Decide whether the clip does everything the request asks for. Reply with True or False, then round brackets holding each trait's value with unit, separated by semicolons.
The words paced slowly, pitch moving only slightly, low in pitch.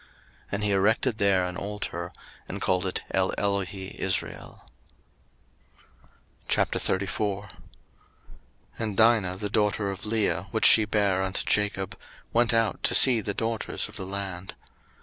True (130 wpm; 2.1 semitones; 100 Hz)